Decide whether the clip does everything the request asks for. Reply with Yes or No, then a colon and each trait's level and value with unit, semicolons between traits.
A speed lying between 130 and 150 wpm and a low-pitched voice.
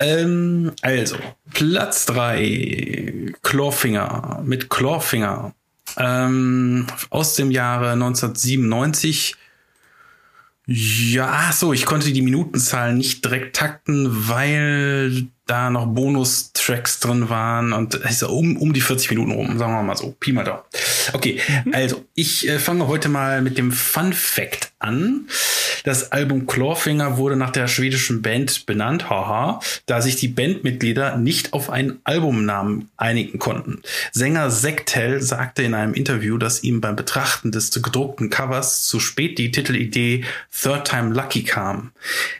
Yes: average, 135 wpm; low, 130 Hz